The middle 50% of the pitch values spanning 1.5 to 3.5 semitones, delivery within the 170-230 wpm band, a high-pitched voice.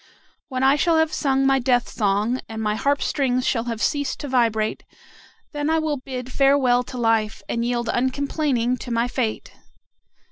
Yes: average, 3.0 semitones; average, 175 wpm; very high, 255 Hz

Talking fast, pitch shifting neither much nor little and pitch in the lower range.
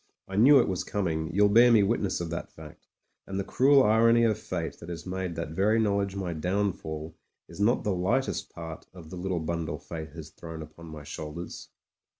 Yes: fast, 210 wpm; average, 4.0 semitones; very low, 90 Hz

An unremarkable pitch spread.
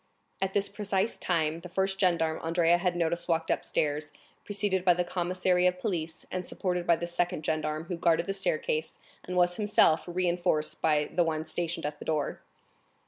No: narrow, 2.2 semitones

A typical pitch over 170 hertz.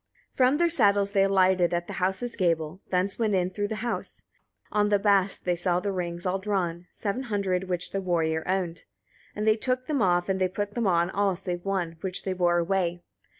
Yes: high, 190 Hz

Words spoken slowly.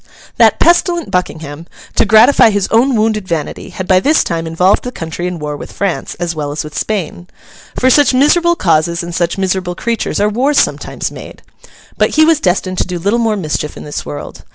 No: average, 200 wpm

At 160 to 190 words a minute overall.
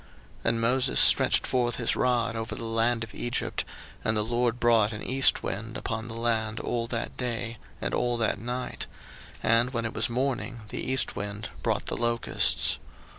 Yes: average, 180 wpm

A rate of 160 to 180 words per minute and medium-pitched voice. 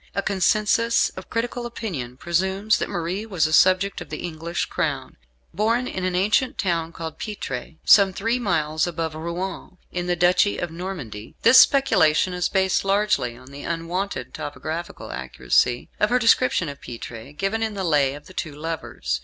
Yes: average, 170 wpm; medium, 180 Hz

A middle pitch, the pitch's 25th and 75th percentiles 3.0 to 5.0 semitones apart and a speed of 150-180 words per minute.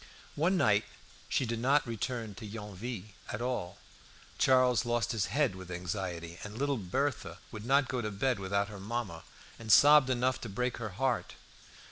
No: low, 115 Hz; average, 4.3 semitones; average, 170 wpm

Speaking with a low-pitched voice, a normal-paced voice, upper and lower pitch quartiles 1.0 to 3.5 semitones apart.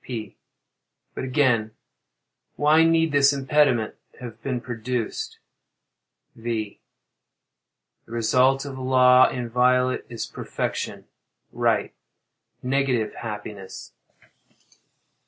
No: low, 125 Hz; slow, 70 wpm; average, 2.7 semitones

